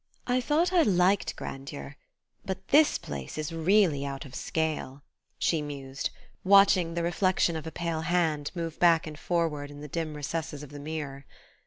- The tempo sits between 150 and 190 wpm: Yes, average, 170 wpm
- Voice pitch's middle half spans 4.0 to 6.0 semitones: No, average, 3.6 semitones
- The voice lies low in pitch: No, medium, 160 Hz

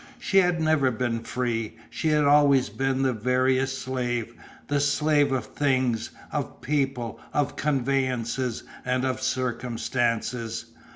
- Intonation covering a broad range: No, average, 2.7 semitones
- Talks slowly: Yes, slow, 125 wpm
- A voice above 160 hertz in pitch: No, low, 130 Hz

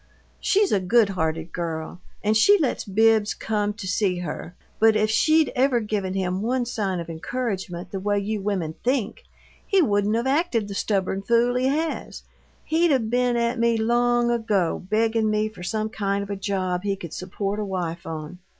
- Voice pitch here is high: Yes, high, 210 Hz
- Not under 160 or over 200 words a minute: Yes, average, 185 wpm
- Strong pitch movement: No, average, 4.0 semitones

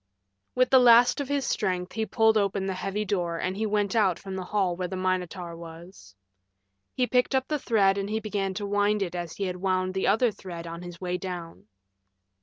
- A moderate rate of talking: No, fast, 215 wpm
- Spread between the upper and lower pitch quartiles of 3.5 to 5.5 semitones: No, average, 2.9 semitones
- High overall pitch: Yes, high, 195 Hz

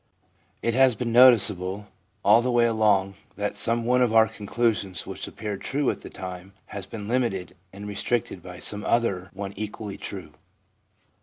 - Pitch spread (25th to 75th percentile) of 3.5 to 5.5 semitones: No, average, 3.1 semitones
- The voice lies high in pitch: No, low, 105 Hz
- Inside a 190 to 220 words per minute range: No, average, 165 wpm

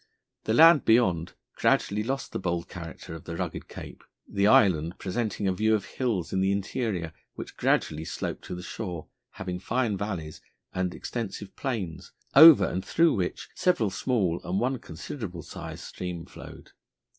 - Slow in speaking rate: No, average, 160 wpm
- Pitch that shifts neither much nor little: Yes, average, 4.5 semitones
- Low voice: Yes, very low, 95 Hz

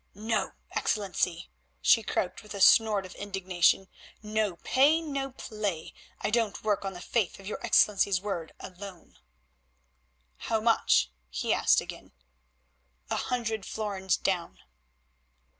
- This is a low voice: No, high, 205 Hz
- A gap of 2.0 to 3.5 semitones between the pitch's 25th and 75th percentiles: Yes, average, 2.8 semitones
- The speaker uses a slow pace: Yes, slow, 125 wpm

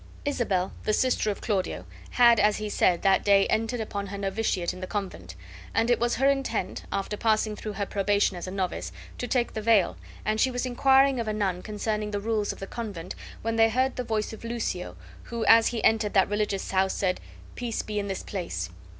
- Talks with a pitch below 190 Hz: No, high, 210 Hz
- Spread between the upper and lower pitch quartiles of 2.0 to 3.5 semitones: Yes, average, 2.9 semitones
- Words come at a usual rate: No, fast, 215 wpm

